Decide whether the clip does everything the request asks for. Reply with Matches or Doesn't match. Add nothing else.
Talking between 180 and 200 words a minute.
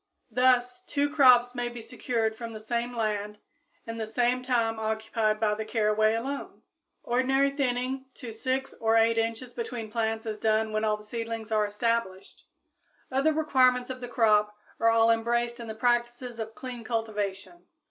Doesn't match